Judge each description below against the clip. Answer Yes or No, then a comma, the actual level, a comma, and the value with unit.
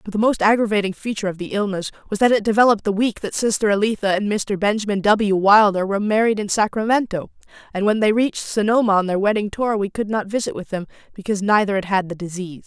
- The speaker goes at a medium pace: No, fast, 225 wpm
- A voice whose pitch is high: Yes, high, 205 Hz